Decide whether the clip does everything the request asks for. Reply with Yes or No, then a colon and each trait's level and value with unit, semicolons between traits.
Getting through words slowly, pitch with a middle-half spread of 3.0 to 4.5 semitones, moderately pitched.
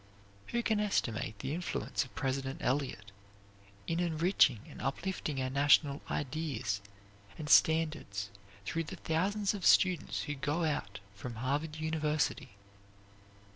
Yes: slow, 125 wpm; average, 4.0 semitones; medium, 150 Hz